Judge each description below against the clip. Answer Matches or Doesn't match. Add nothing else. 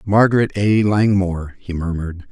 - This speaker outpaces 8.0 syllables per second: Doesn't match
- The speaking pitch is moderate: Doesn't match